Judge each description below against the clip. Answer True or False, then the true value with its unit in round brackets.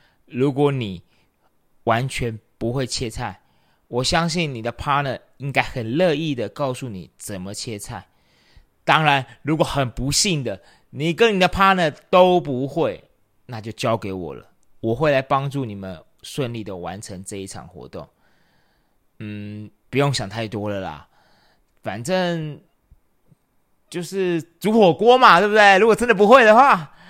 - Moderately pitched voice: False (130 Hz)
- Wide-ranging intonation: True (7.6 semitones)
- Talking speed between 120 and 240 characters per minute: True (235 characters per minute)